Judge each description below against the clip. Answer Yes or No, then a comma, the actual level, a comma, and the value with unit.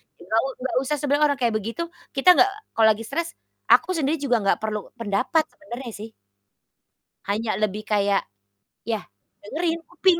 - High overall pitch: Yes, high, 245 Hz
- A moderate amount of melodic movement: No, wide, 6.4 semitones